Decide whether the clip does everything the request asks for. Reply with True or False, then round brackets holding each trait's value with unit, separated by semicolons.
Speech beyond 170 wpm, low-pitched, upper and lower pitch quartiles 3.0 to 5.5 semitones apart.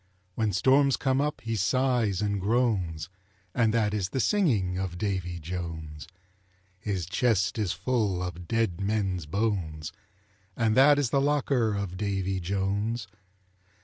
False (140 wpm; 100 Hz; 4.3 semitones)